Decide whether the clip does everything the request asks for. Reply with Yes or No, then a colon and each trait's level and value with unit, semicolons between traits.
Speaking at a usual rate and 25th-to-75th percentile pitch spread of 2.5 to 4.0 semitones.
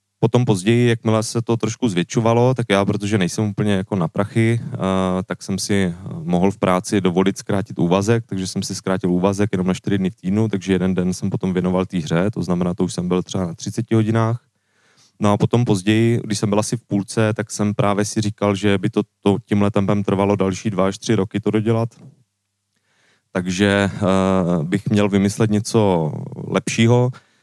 No: fast, 195 wpm; average, 2.8 semitones